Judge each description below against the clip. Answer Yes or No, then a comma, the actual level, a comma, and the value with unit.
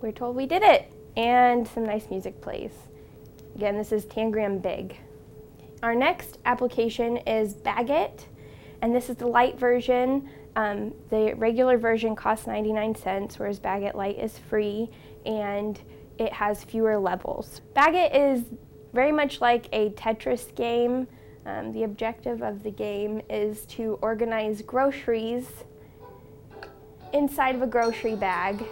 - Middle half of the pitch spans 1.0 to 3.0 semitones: Yes, narrow, 2.5 semitones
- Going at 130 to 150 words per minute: Yes, average, 140 wpm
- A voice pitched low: No, high, 225 Hz